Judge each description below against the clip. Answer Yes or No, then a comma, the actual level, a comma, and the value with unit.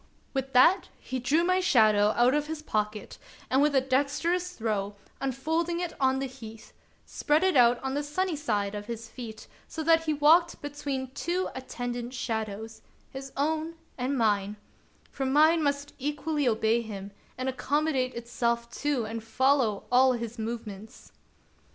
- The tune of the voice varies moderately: Yes, average, 4.5 semitones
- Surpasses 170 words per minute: No, average, 165 wpm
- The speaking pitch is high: Yes, very high, 260 Hz